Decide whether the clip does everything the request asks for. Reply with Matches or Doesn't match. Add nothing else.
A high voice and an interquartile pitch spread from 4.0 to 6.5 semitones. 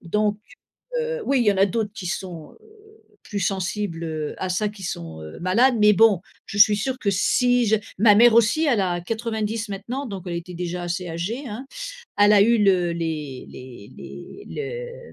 Matches